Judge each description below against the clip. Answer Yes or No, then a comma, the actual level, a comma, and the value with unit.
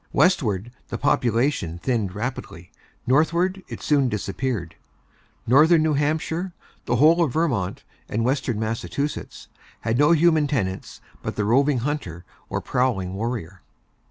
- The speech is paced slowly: Yes, slow, 130 wpm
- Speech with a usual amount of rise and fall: No, wide, 6.1 semitones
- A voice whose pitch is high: No, low, 125 Hz